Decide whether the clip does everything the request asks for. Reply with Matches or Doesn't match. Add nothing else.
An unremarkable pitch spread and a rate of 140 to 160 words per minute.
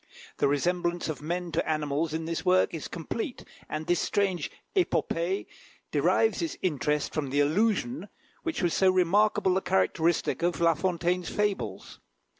Matches